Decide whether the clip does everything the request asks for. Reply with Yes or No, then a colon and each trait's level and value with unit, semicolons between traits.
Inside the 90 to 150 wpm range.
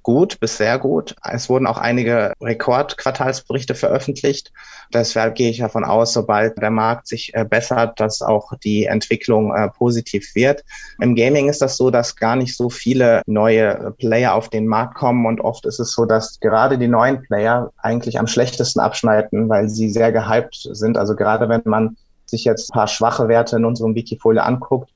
No: average, 180 wpm